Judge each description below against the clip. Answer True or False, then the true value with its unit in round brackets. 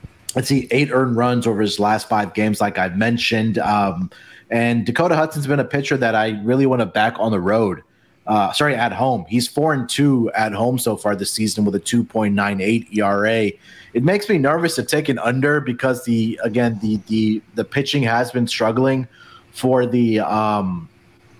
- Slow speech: False (200 wpm)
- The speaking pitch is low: True (115 Hz)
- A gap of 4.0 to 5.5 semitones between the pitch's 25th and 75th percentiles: False (3.4 semitones)